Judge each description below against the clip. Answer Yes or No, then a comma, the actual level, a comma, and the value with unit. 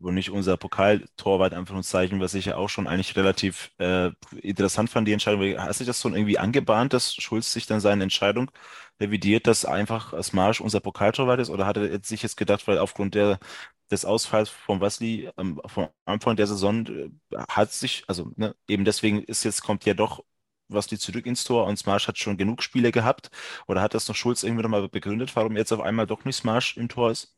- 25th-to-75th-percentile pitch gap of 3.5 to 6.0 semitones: No, narrow, 2.4 semitones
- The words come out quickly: Yes, fast, 215 wpm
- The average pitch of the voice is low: Yes, low, 105 Hz